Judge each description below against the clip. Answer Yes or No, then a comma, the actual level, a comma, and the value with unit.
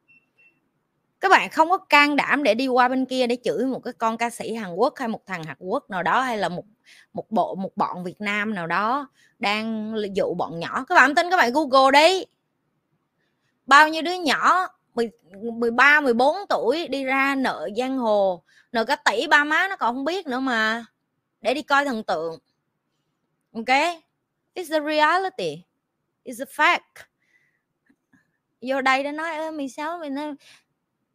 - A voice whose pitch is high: Yes, very high, 260 Hz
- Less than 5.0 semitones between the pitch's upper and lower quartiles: No, average, 5.3 semitones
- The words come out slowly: No, average, 175 wpm